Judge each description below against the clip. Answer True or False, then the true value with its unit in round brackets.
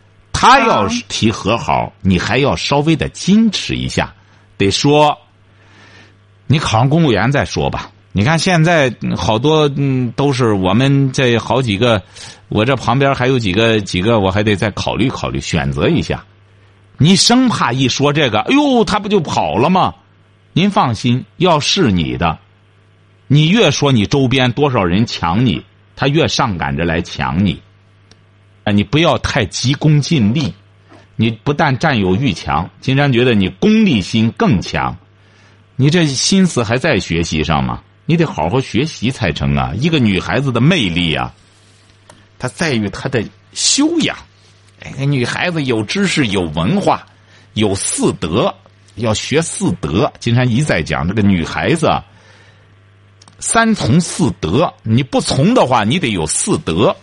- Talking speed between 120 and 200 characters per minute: False (215 characters per minute)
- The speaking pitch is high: False (110 Hz)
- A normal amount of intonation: False (6.6 semitones)